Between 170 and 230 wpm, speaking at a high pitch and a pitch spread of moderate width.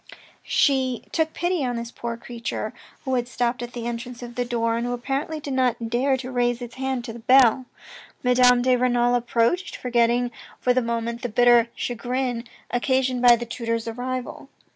No: average, 185 wpm; high, 245 Hz; narrow, 1.4 semitones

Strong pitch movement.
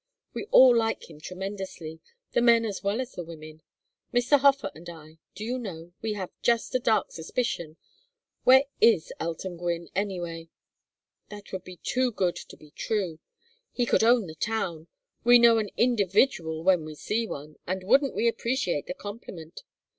Yes: wide, 5.8 semitones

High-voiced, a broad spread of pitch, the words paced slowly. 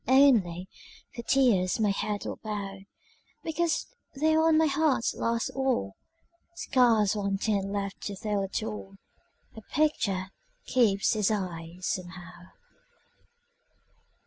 No: high, 210 Hz; average, 5.0 semitones; slow, 120 wpm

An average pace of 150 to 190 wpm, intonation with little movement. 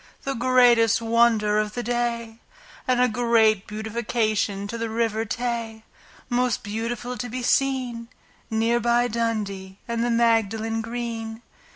No: slow, 135 wpm; narrow, 1.5 semitones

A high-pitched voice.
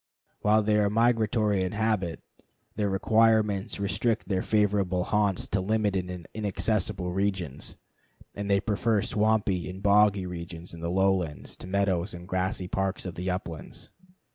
No: low, 100 Hz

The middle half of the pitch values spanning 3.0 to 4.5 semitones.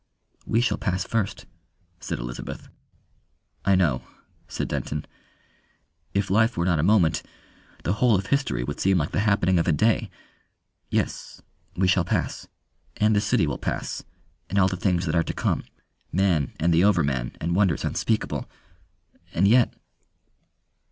Yes: average, 3.8 semitones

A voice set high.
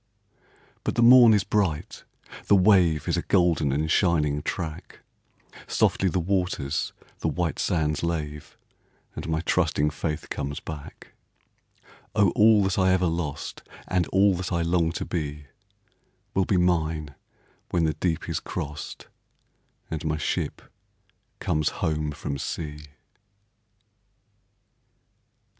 No: very low, 80 Hz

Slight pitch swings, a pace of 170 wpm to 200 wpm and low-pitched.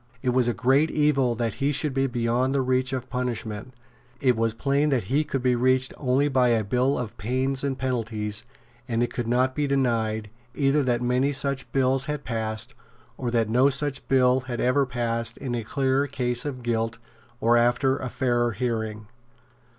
Yes: narrow, 2.3 semitones; average, 190 wpm; low, 125 Hz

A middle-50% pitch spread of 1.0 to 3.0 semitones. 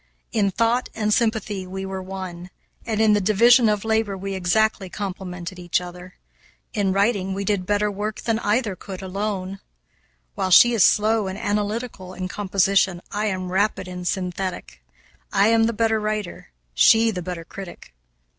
Yes: narrow, 2.6 semitones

